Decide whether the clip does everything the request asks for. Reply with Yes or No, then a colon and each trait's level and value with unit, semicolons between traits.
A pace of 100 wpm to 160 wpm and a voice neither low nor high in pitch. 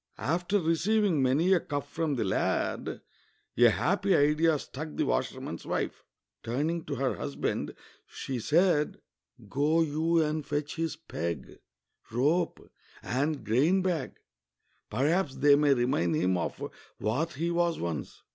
Yes: slow, 135 wpm; medium, 150 Hz